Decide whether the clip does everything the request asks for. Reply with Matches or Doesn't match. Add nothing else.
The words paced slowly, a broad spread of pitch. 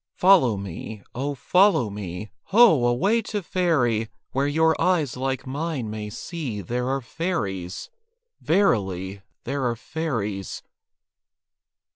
Matches